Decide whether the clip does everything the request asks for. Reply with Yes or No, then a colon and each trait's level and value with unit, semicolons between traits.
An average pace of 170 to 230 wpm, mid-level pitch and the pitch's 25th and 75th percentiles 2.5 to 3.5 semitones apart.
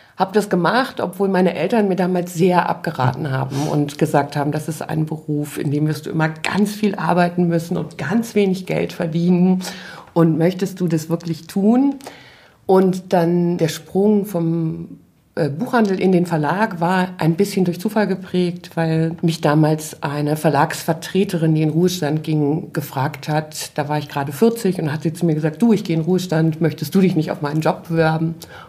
Yes: average, 185 wpm; medium, 170 Hz; average, 2.9 semitones